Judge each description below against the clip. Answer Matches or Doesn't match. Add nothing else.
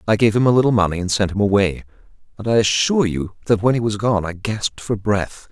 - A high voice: Doesn't match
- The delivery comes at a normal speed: Doesn't match